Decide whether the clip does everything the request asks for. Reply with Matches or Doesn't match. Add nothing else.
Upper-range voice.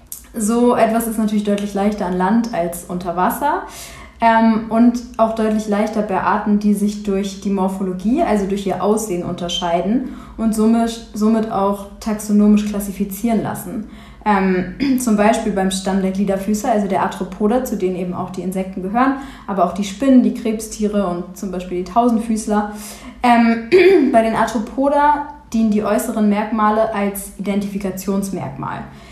Matches